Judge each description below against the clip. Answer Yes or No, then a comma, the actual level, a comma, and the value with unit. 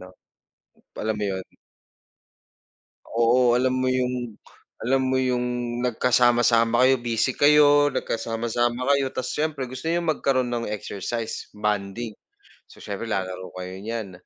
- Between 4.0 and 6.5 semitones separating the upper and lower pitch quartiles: No, narrow, 2.6 semitones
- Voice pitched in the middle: No, low, 120 Hz